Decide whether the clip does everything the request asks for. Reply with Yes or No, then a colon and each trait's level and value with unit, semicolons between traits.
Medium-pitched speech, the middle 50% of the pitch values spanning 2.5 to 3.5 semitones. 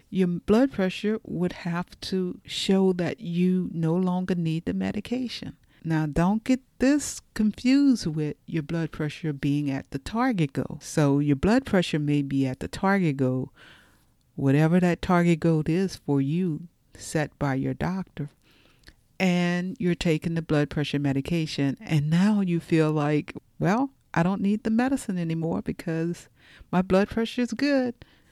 No: medium, 170 Hz; average, 4.4 semitones